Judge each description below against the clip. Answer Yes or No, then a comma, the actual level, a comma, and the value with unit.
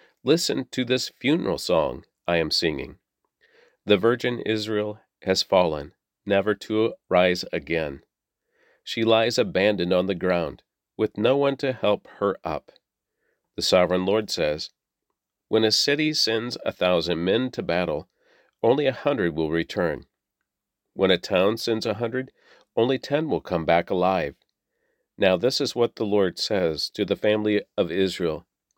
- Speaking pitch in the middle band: No, low, 105 Hz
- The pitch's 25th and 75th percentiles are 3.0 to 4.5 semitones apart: Yes, average, 3.8 semitones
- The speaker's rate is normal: Yes, average, 150 wpm